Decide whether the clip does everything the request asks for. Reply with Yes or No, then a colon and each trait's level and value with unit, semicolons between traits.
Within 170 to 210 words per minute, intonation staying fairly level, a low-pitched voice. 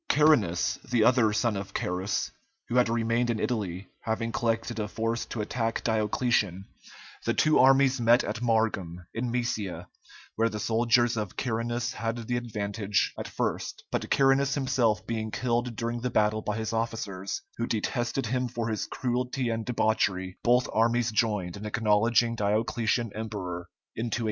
No: average, 160 wpm; narrow, 2.1 semitones; low, 115 Hz